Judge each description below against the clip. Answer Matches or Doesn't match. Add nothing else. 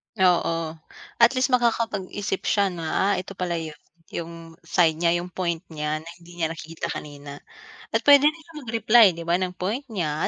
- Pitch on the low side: Doesn't match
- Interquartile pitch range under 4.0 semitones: Doesn't match